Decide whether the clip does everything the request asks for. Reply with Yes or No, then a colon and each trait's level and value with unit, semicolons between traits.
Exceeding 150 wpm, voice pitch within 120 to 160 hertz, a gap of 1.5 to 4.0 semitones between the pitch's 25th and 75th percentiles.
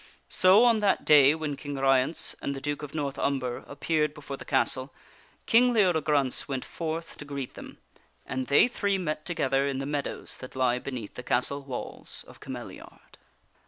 Yes: average, 180 wpm; medium, 140 Hz; average, 2.9 semitones